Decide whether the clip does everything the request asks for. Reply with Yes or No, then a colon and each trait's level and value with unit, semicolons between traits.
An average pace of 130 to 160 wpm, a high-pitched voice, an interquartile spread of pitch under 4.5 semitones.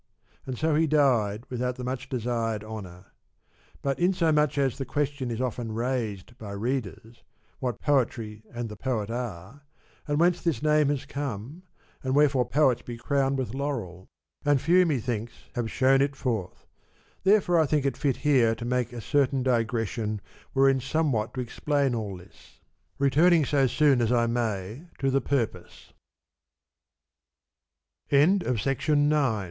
No: average, 145 wpm; low, 130 Hz; average, 3.9 semitones